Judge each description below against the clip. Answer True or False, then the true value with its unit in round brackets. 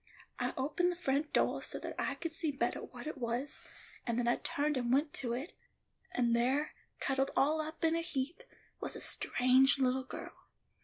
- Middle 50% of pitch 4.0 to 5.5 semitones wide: False (3.5 semitones)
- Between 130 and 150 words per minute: False (195 wpm)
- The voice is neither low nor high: False (270 Hz)